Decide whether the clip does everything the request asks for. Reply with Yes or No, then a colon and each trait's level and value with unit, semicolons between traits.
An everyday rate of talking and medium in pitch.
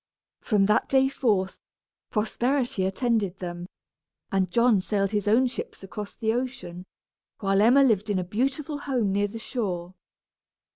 No: average, 145 wpm; high, 210 Hz